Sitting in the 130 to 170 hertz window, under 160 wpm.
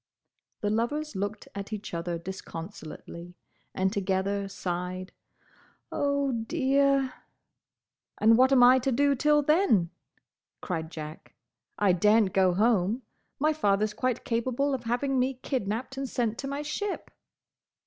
No: high, 225 Hz; average, 140 wpm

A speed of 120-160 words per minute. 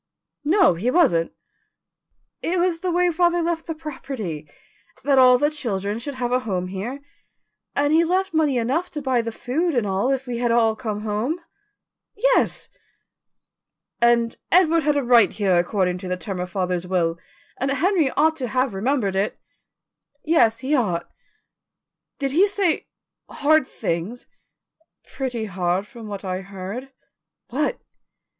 Yes: average, 155 wpm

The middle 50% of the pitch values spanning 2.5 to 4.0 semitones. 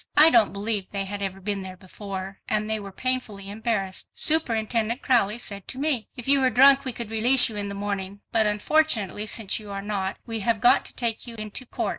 Yes: average, 3.2 semitones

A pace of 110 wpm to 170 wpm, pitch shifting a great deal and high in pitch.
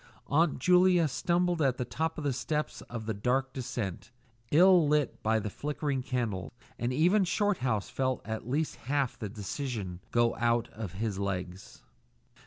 No: average, 150 wpm; wide, 5.7 semitones; low, 130 Hz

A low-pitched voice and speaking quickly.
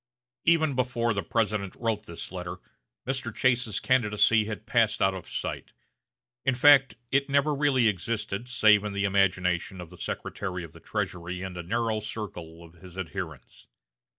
No: low, 105 Hz; average, 160 wpm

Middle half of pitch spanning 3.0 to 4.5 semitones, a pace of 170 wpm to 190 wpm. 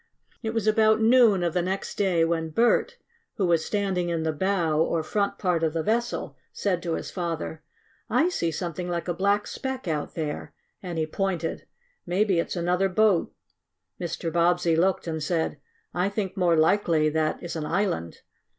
Yes: average, 3.4 semitones; average, 180 wpm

